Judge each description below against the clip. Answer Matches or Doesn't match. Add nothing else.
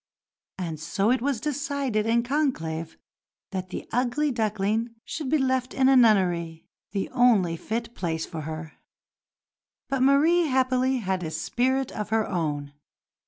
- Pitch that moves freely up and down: Matches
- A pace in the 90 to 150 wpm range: Matches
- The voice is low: Doesn't match